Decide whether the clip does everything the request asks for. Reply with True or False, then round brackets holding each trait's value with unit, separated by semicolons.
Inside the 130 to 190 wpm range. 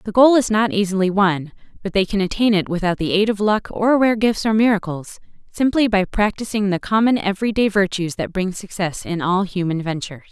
False (200 wpm)